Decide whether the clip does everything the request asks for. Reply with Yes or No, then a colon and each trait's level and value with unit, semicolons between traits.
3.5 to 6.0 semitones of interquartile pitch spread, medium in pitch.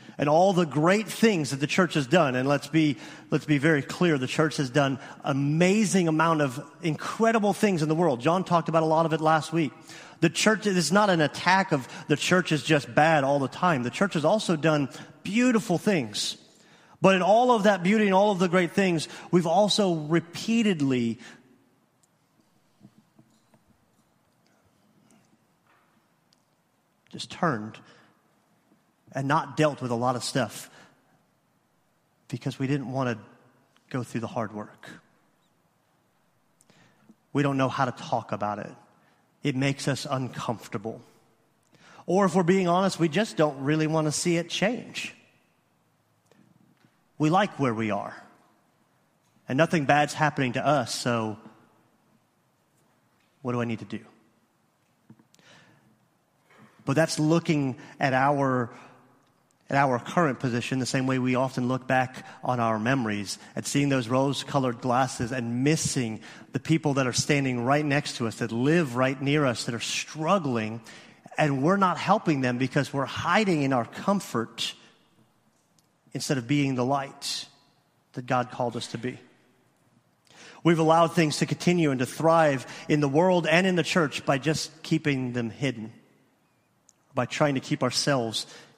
Yes: average, 4.6 semitones; medium, 145 Hz